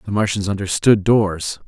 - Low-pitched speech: Yes, low, 100 Hz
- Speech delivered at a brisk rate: No, average, 145 wpm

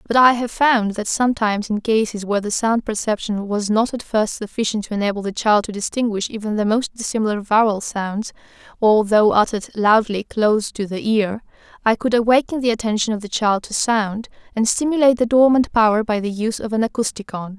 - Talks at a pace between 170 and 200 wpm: Yes, average, 195 wpm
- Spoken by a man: No, female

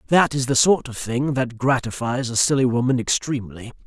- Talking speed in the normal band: Yes, average, 185 wpm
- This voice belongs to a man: Yes, male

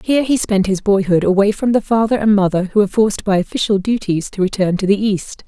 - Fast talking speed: Yes, fast, 240 wpm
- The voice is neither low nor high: No, high, 205 Hz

